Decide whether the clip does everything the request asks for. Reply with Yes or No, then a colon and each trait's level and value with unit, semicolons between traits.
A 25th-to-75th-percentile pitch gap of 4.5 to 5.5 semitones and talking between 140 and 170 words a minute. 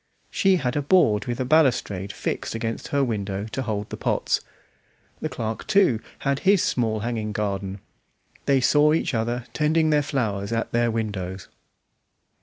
Yes: average, 5.1 semitones; average, 160 wpm